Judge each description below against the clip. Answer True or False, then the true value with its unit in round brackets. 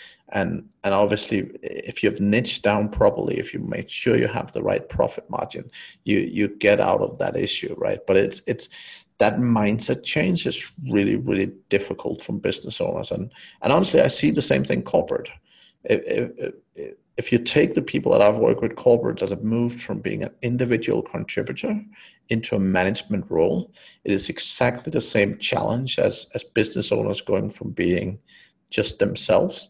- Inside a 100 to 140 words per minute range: False (175 wpm)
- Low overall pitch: False (180 Hz)